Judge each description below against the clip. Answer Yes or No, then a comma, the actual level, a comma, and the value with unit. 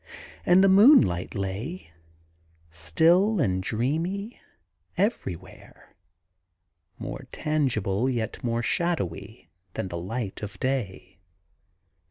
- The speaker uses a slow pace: Yes, slow, 90 wpm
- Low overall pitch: Yes, low, 120 Hz